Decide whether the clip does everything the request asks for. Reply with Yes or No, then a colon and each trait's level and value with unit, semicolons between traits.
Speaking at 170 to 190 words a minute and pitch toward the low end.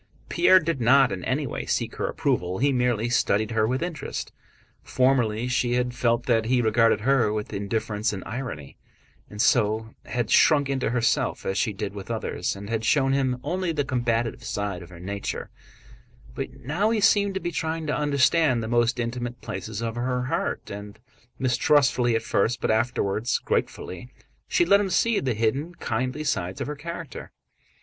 Yes: average, 180 wpm; low, 120 Hz